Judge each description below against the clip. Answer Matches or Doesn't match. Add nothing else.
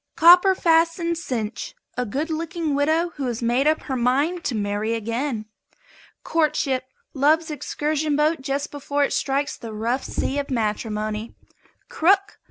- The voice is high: Matches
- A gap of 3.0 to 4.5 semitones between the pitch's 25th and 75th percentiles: Doesn't match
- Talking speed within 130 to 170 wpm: Matches